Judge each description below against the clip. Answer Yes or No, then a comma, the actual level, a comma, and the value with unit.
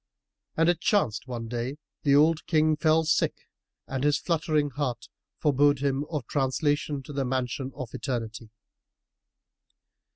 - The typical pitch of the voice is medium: Yes, medium, 145 Hz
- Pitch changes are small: No, average, 3.1 semitones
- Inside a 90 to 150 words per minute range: Yes, average, 140 wpm